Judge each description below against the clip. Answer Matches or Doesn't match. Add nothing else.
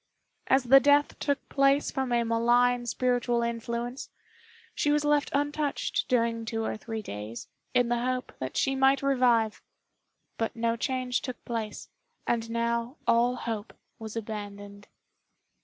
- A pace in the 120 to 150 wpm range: Matches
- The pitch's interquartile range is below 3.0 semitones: Matches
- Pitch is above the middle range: Matches